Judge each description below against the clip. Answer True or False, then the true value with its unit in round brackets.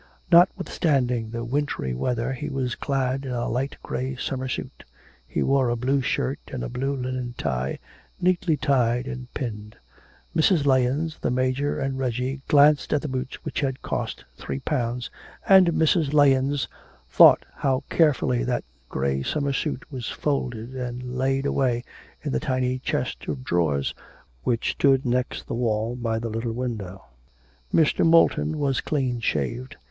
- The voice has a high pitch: False (130 Hz)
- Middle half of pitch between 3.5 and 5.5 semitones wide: False (2.7 semitones)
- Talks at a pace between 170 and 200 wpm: False (155 wpm)